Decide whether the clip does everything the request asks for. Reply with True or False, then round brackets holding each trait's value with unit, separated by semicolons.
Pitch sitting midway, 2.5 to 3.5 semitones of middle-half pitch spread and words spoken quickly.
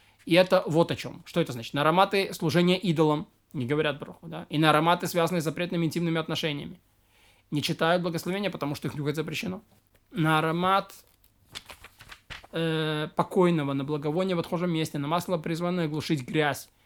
True (160 Hz; 2.8 semitones; 165 wpm)